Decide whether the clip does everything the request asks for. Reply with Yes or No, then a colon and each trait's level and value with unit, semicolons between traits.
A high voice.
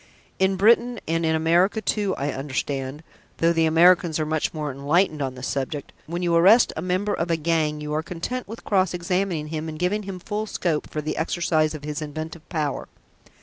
No: medium, 165 Hz